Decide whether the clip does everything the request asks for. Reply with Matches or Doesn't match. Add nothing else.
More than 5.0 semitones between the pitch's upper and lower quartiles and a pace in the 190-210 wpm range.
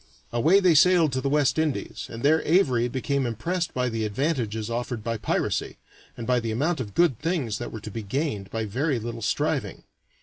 Matches